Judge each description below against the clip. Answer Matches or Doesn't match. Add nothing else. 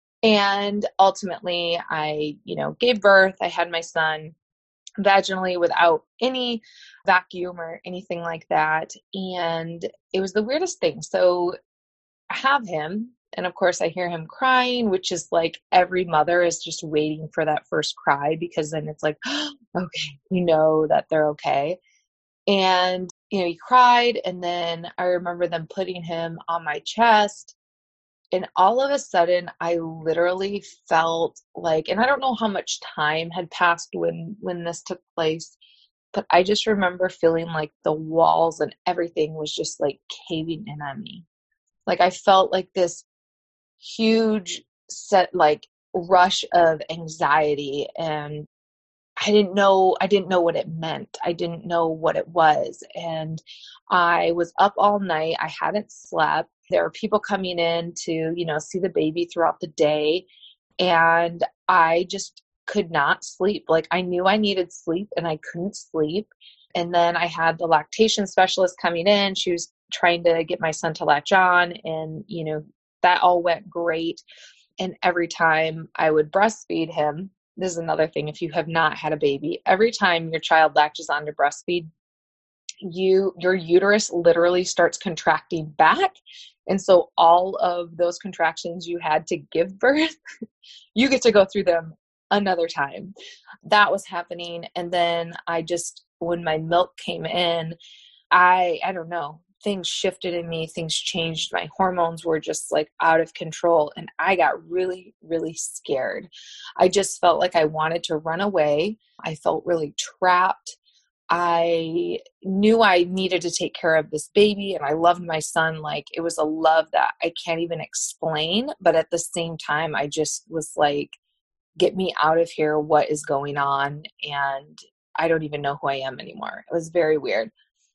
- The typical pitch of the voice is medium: Matches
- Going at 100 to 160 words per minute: Doesn't match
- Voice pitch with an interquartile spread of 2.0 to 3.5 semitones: Matches